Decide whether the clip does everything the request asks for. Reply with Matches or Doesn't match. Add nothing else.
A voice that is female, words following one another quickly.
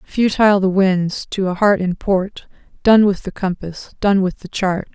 Doesn't match